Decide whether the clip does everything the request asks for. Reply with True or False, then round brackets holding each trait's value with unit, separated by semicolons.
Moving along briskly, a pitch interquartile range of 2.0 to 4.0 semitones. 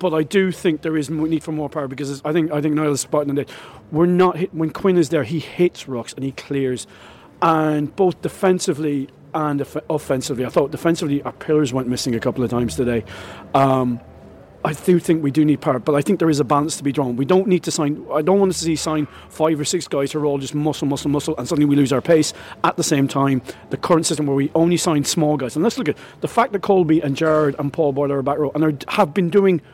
True (260 wpm; 2.9 semitones)